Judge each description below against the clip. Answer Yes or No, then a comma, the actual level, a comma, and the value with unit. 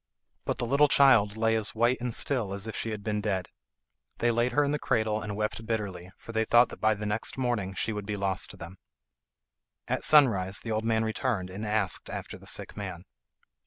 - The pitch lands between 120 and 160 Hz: No, low, 110 Hz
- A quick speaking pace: Yes, fast, 220 wpm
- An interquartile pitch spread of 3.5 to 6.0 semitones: No, narrow, 2.5 semitones